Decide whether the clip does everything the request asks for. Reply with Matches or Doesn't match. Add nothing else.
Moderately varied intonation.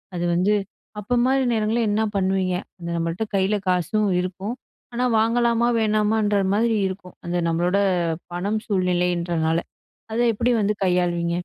Matches